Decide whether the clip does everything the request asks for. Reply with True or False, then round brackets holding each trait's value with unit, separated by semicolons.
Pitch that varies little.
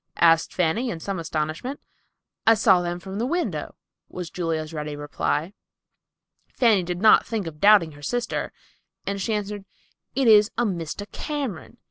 False (5.2 semitones)